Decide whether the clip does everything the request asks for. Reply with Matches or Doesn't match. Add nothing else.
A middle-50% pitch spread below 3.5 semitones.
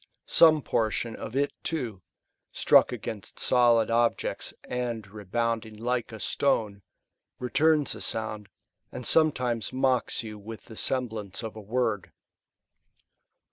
Matches